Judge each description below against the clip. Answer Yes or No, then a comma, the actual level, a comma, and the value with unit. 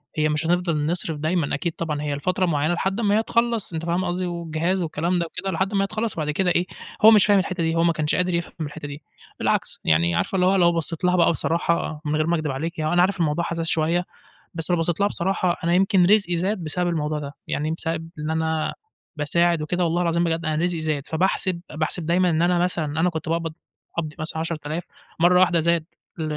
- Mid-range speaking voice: Yes, medium, 170 Hz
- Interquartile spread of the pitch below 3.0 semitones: Yes, narrow, 2.4 semitones